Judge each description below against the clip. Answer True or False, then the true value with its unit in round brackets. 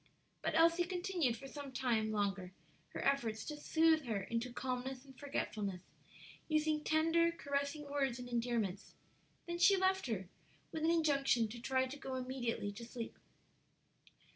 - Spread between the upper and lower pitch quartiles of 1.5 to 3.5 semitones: False (5.1 semitones)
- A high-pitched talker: True (265 Hz)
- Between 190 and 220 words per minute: False (150 wpm)